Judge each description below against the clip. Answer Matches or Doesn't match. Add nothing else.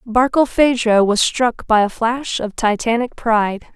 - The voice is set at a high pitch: Matches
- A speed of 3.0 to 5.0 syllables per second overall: Matches